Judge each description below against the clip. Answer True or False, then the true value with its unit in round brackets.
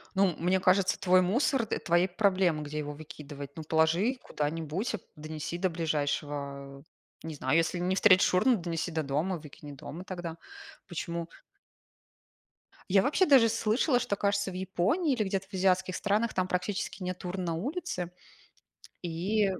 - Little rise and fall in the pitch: False (3.8 semitones)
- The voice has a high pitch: False (180 Hz)